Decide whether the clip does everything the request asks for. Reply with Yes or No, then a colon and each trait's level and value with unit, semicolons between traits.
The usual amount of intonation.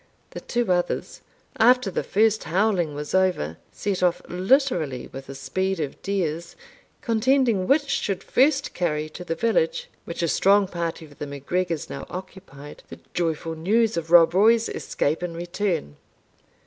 Yes: average, 4.6 semitones